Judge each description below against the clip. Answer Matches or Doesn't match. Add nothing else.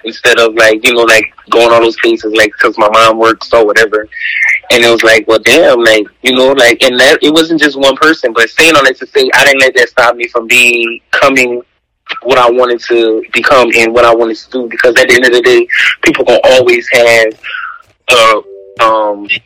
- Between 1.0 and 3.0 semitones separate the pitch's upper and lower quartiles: Matches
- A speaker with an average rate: Doesn't match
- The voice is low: Matches